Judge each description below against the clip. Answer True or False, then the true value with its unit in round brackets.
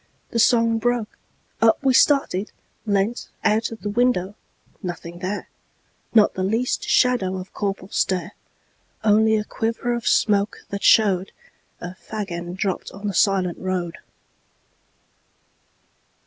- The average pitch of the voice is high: True (205 Hz)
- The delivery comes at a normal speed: False (110 wpm)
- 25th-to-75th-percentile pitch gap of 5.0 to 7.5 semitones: False (3.3 semitones)